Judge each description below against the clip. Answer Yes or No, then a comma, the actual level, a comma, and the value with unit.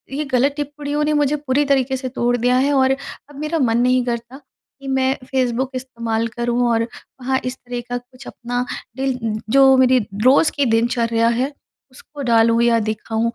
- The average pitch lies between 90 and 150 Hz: No, very high, 255 Hz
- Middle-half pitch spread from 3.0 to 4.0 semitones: No, narrow, 2.4 semitones